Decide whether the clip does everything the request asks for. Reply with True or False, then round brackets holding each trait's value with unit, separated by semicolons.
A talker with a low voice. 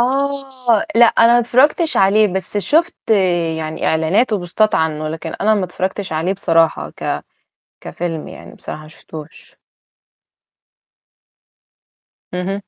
False (195 Hz)